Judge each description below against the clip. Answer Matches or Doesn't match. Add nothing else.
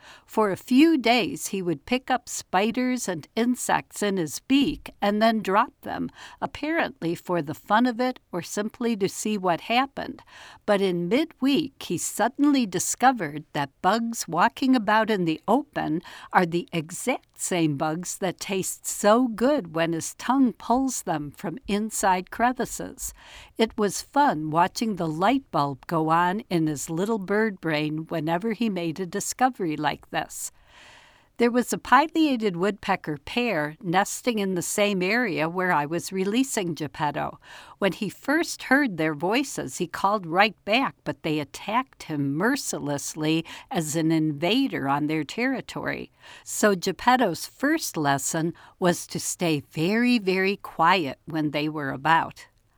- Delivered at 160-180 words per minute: Doesn't match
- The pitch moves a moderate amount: Doesn't match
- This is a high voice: Matches